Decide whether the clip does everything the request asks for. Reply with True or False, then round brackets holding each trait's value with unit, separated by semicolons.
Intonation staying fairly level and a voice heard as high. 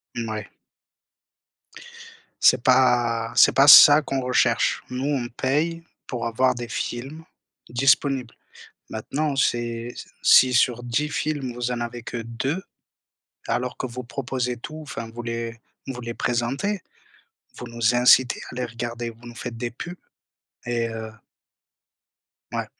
False (2.3 semitones; 120 Hz)